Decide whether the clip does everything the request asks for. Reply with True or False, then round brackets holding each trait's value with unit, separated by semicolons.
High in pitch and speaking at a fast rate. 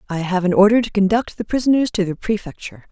True (200 Hz; 225 wpm)